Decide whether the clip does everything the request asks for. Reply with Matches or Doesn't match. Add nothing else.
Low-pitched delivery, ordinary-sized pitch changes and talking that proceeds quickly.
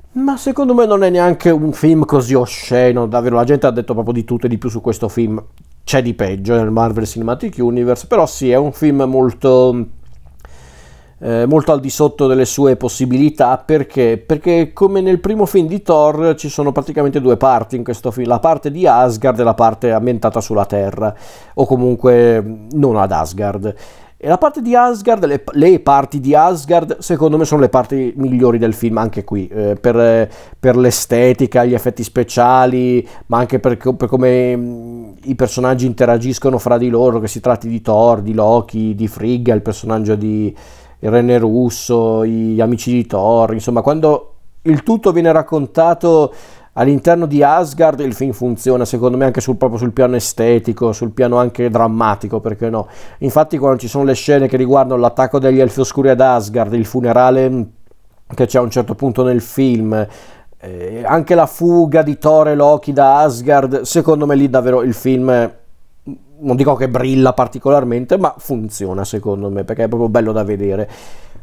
Matches